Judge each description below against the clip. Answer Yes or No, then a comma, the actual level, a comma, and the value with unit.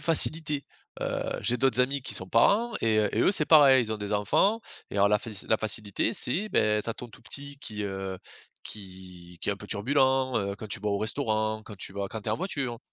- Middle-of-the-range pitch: No, low, 110 Hz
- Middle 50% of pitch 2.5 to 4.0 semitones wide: No, average, 4.8 semitones